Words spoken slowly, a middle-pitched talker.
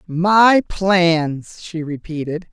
Yes: slow, 95 wpm; medium, 170 Hz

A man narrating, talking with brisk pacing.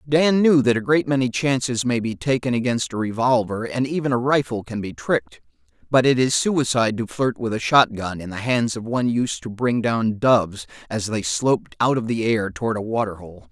Yes: male; fast, 220 wpm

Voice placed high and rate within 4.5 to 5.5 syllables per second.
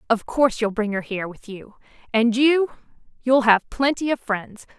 Yes: high, 235 Hz; 4.9 syllables/s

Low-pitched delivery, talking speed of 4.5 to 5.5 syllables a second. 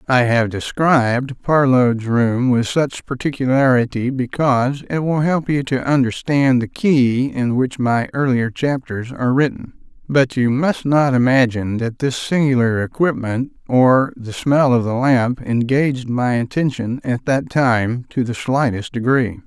No: low, 130 Hz; 4.2 syllables/s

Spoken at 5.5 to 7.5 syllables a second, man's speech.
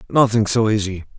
Yes: 5.6 syllables/s; male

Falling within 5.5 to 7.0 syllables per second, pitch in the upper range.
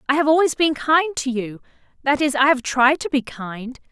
No: 5.0 syllables/s; very high, 270 Hz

